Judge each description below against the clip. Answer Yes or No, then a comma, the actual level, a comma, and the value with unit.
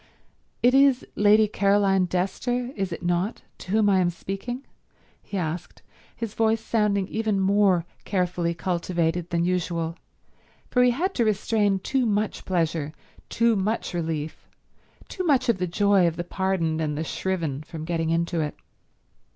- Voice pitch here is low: No, high, 190 Hz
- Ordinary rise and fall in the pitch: Yes, average, 4.2 semitones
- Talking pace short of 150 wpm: No, average, 155 wpm